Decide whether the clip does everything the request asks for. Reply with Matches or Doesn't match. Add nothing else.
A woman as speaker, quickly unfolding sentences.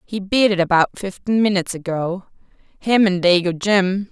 Doesn't match